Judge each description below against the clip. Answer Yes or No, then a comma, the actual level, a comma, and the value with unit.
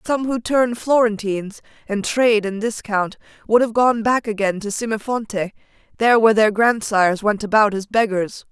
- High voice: Yes, high, 215 Hz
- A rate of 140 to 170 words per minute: Yes, average, 160 wpm